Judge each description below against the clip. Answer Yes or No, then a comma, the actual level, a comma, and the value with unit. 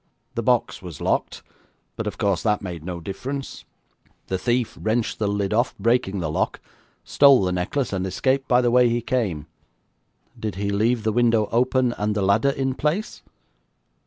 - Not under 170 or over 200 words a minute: Yes, average, 175 wpm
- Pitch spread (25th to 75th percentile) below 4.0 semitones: No, average, 4.3 semitones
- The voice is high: No, low, 110 Hz